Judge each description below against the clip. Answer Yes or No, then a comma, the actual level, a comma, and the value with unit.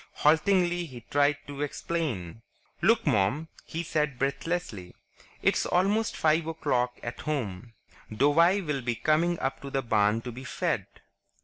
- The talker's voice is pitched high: No, medium, 145 Hz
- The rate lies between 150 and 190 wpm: No, average, 140 wpm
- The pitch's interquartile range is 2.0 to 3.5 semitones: No, wide, 5.5 semitones